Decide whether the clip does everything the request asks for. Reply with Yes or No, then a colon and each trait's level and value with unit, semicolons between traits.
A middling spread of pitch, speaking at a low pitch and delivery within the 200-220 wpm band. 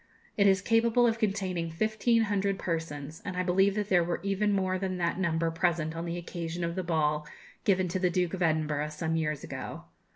No: average, 3.1 semitones; medium, 180 Hz; fast, 205 wpm